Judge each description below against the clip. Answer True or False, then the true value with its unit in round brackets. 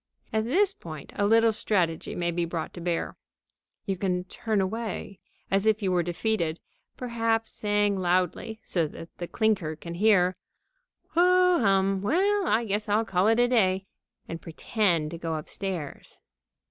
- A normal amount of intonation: True (4.2 semitones)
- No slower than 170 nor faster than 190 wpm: False (160 wpm)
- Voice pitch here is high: True (195 Hz)